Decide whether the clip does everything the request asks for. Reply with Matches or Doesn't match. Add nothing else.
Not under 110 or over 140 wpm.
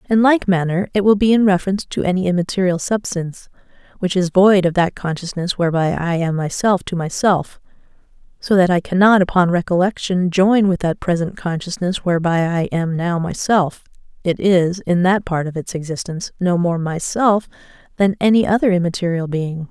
Doesn't match